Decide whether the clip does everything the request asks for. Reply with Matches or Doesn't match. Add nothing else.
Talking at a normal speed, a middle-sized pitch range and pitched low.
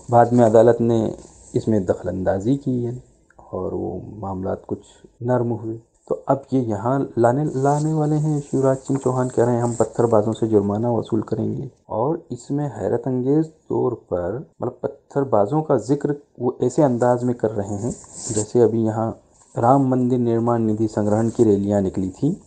Matches